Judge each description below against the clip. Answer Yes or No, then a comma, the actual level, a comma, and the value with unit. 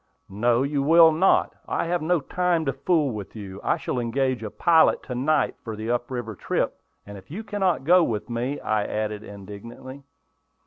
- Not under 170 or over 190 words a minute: Yes, average, 185 wpm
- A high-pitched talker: No, low, 130 Hz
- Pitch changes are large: Yes, wide, 6.7 semitones